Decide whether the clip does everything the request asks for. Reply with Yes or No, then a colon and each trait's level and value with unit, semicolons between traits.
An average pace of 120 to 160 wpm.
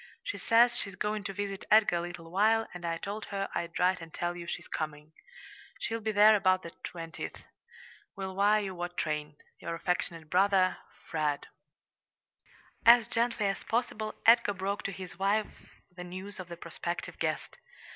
No: average, 170 wpm